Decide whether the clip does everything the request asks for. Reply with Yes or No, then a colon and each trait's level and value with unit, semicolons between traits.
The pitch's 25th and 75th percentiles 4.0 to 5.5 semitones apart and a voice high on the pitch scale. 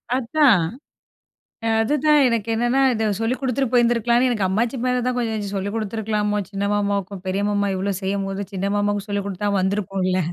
No: average, 3.2 semitones; high, 210 Hz